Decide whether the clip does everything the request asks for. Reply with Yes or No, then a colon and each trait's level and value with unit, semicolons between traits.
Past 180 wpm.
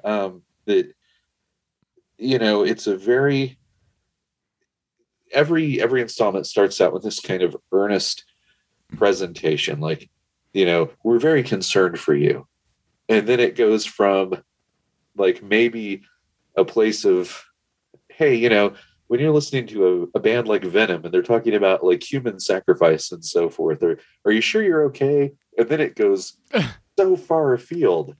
No: average, 150 wpm